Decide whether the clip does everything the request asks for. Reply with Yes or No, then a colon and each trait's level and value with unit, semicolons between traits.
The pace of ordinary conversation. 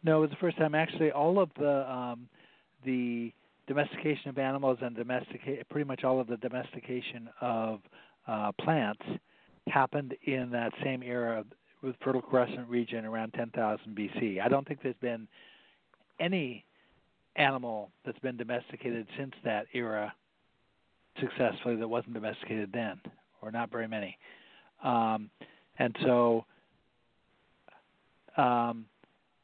No: slow, 130 wpm